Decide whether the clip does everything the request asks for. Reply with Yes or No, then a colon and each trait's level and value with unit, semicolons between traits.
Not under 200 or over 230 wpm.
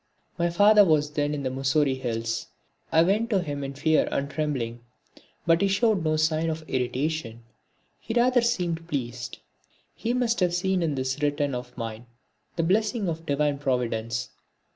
No: average, 165 wpm